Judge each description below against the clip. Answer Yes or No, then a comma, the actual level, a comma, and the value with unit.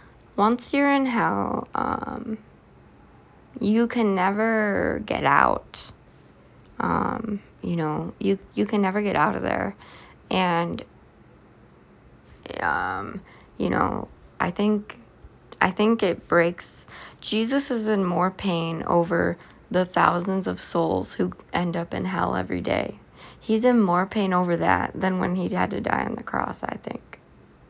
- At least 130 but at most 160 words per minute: Yes, average, 140 wpm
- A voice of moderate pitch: No, high, 195 Hz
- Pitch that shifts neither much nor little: Yes, average, 4.0 semitones